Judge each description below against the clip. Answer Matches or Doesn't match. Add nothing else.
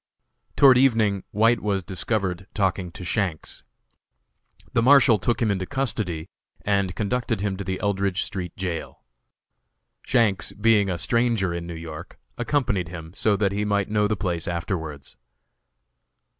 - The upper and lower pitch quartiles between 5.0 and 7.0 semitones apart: Doesn't match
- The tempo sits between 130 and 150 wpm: Matches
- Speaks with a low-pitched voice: Matches